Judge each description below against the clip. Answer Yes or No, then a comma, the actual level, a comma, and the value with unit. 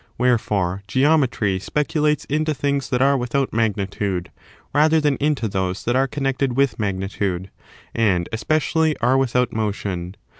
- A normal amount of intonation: No, wide, 6.1 semitones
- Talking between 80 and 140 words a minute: Yes, slow, 135 wpm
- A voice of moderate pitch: No, low, 125 Hz